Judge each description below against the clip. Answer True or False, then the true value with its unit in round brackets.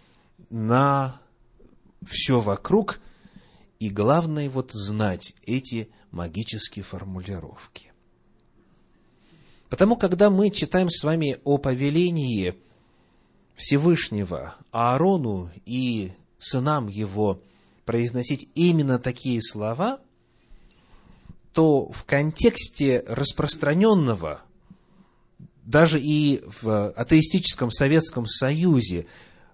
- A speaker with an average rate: False (75 wpm)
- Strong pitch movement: True (6.5 semitones)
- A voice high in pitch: False (130 Hz)